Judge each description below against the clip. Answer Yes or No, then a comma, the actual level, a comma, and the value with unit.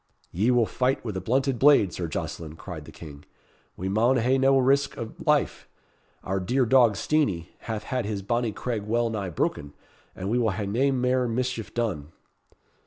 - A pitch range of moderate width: Yes, average, 4.9 semitones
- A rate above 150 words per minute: Yes, average, 180 wpm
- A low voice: Yes, low, 115 Hz